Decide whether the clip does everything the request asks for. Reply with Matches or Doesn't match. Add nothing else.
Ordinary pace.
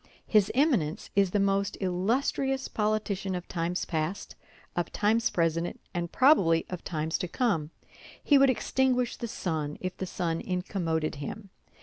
Matches